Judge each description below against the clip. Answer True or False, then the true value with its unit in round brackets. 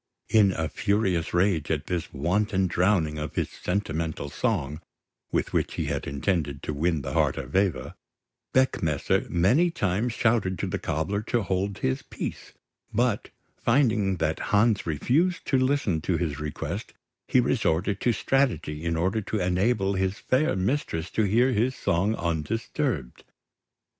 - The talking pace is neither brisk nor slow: True (150 wpm)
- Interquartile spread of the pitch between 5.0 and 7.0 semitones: True (5.6 semitones)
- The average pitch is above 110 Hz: False (95 Hz)